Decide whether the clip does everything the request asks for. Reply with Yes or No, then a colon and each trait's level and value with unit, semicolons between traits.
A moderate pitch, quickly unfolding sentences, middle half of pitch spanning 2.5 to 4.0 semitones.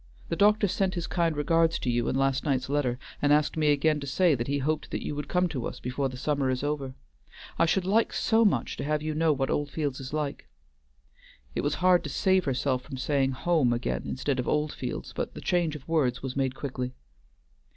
Yes: medium, 145 Hz; fast, 225 wpm; average, 3.6 semitones